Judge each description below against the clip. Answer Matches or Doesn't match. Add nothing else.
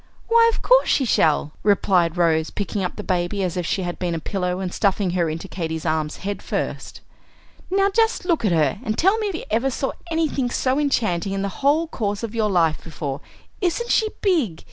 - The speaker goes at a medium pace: Doesn't match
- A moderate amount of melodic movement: Doesn't match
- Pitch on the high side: Matches